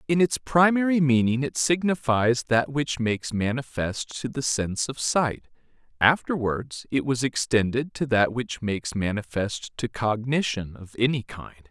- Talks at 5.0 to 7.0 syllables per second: No, 4.5 syllables/s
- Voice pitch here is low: Yes, low, 125 Hz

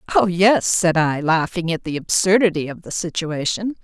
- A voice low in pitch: No, medium, 180 Hz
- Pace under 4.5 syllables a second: No, 4.7 syllables/s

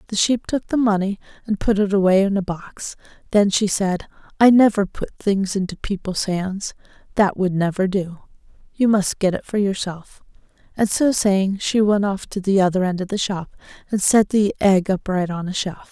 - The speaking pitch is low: No, high, 195 Hz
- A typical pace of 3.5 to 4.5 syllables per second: No, 4.8 syllables/s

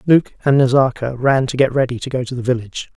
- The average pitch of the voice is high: No, low, 130 Hz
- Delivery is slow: No, fast, 240 wpm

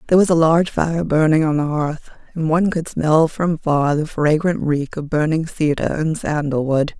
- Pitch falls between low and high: Yes, medium, 155 Hz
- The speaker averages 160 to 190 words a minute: No, fast, 205 wpm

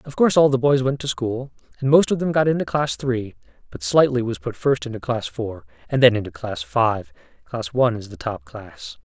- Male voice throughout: Yes, male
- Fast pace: Yes, fast, 230 wpm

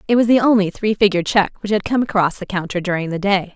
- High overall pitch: Yes, high, 200 Hz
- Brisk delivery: Yes, fast, 270 wpm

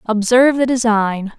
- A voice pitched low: No, high, 230 Hz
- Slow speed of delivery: Yes, slow, 130 wpm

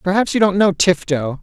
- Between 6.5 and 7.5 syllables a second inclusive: No, 5.3 syllables/s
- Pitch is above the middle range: No, medium, 180 Hz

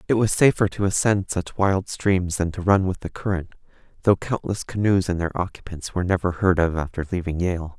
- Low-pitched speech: Yes, very low, 90 Hz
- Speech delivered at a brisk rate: Yes, fast, 210 wpm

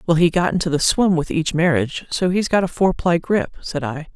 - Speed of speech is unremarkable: No, fast, 245 wpm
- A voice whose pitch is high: No, medium, 170 Hz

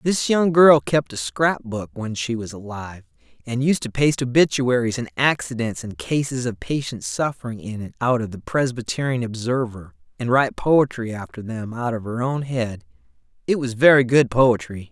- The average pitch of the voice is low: Yes, low, 120 Hz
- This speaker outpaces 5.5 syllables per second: No, 5.0 syllables/s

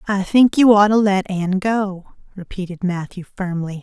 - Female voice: Yes, female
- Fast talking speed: No, average, 170 wpm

